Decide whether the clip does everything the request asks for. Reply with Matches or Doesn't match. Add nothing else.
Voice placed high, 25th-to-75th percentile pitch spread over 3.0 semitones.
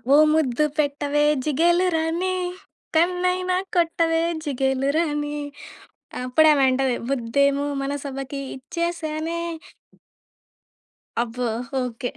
Matches